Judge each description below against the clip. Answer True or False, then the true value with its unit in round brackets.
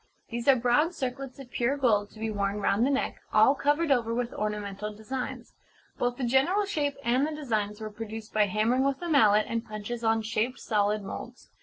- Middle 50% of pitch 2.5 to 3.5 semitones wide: False (4.0 semitones)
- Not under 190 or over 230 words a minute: True (200 wpm)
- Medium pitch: False (235 Hz)